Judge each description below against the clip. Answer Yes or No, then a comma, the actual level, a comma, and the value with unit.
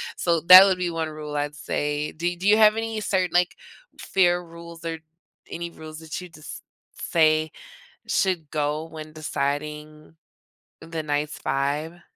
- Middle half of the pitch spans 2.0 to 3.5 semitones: Yes, narrow, 2.5 semitones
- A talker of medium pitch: Yes, medium, 160 Hz